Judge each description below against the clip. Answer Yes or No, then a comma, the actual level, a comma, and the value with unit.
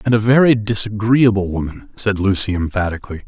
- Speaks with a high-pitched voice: No, low, 105 Hz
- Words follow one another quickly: No, average, 145 wpm